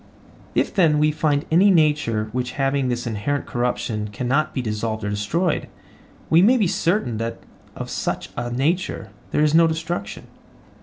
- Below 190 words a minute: Yes, average, 160 wpm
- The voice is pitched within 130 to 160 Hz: Yes, medium, 140 Hz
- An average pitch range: No, wide, 5.7 semitones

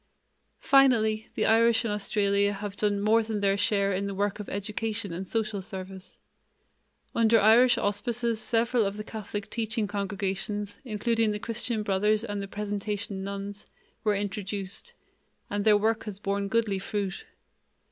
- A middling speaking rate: Yes, average, 150 wpm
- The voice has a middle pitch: No, high, 210 Hz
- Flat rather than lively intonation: Yes, narrow, 1.9 semitones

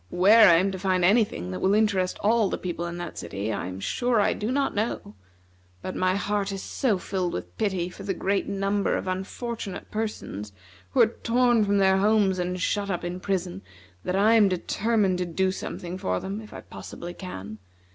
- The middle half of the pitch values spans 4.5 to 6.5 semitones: No, average, 2.8 semitones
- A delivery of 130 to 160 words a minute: No, fast, 205 wpm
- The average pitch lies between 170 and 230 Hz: Yes, high, 190 Hz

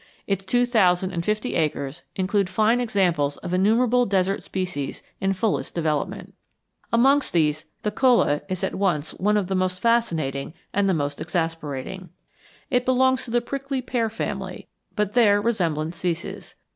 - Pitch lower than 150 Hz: No, high, 190 Hz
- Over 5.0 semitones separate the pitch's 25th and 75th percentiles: Yes, wide, 5.5 semitones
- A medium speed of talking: Yes, average, 155 wpm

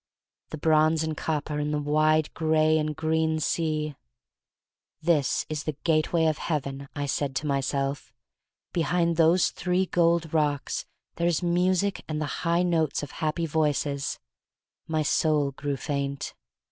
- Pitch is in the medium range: Yes, medium, 155 Hz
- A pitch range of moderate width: No, narrow, 1.9 semitones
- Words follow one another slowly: No, average, 145 wpm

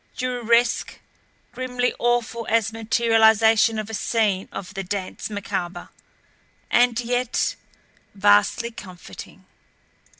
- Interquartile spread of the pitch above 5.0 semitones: No, average, 2.9 semitones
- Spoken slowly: Yes, slow, 95 wpm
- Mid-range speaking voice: No, high, 225 Hz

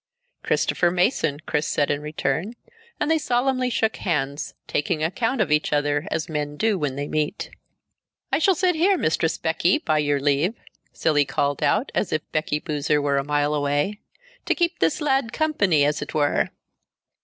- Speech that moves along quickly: No, average, 175 wpm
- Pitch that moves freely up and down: Yes, wide, 7.4 semitones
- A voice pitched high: No, medium, 155 Hz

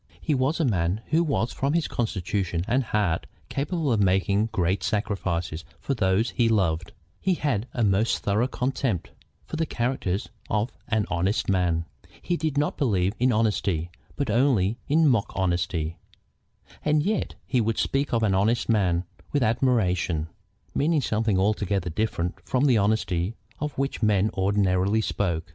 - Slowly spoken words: No, average, 155 wpm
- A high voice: No, low, 105 Hz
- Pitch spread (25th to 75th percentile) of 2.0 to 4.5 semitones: No, wide, 5.5 semitones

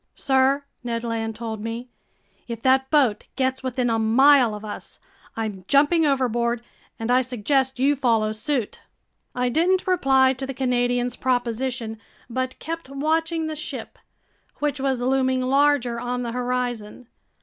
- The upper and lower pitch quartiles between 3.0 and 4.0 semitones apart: No, narrow, 2.6 semitones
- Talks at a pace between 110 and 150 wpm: Yes, average, 145 wpm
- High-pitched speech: Yes, very high, 255 Hz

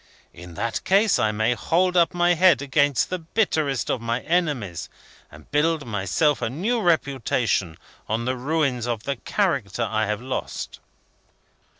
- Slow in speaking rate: No, average, 155 wpm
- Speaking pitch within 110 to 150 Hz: Yes, low, 135 Hz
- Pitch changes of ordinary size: No, wide, 6.8 semitones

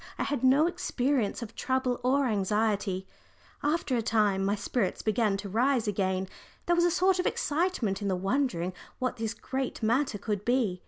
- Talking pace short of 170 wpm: No, average, 175 wpm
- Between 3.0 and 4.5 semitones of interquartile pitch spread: No, average, 5.0 semitones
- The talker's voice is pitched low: No, high, 230 Hz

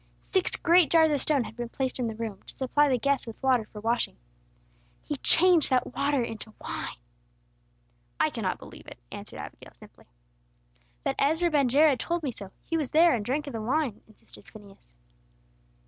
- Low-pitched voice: No, very high, 265 Hz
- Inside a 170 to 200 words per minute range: Yes, average, 185 wpm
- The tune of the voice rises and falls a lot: No, average, 4.9 semitones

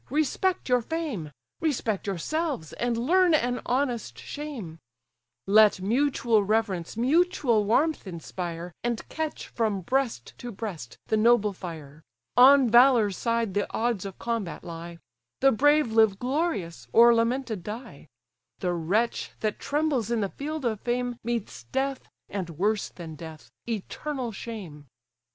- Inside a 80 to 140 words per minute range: Yes, slow, 135 wpm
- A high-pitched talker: Yes, high, 230 Hz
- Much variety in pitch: Yes, wide, 5.7 semitones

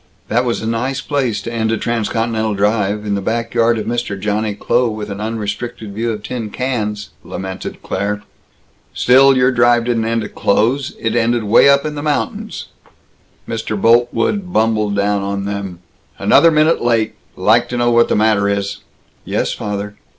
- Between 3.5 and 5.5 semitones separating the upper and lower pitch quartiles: No, narrow, 2.5 semitones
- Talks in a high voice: No, low, 115 Hz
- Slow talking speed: No, average, 175 wpm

